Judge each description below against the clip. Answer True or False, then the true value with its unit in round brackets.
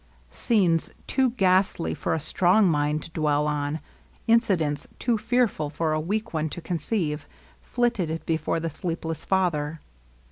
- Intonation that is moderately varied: True (4.5 semitones)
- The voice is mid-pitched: True (165 Hz)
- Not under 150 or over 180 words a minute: False (140 wpm)